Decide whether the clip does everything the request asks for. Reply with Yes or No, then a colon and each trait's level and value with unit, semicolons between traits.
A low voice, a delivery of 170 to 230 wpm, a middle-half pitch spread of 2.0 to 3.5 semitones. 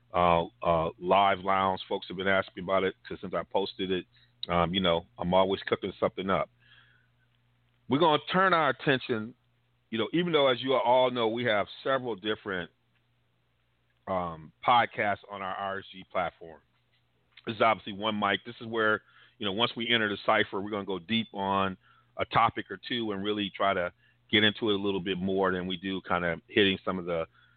No: low, 100 Hz; average, 200 wpm; average, 4.2 semitones